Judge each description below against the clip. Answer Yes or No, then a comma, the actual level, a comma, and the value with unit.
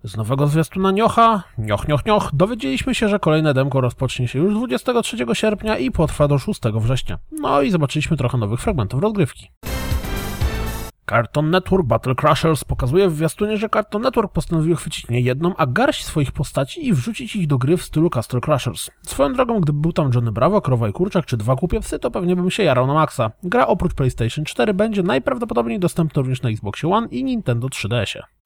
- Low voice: No, medium, 155 Hz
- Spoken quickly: Yes, fast, 190 wpm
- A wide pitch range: Yes, wide, 8.1 semitones